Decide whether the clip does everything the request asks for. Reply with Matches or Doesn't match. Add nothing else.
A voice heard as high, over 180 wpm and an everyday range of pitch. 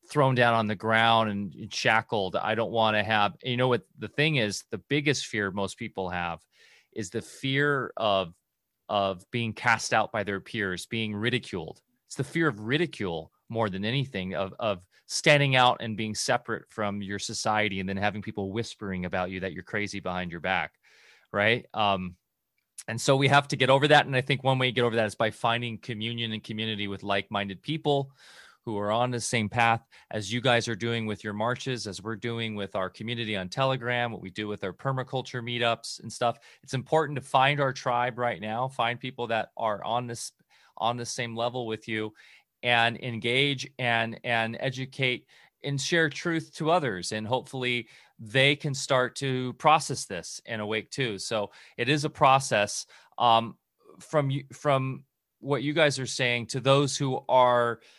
Doesn't match